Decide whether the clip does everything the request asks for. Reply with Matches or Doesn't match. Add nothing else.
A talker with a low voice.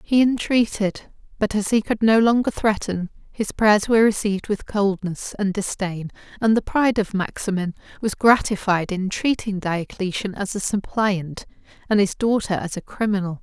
Doesn't match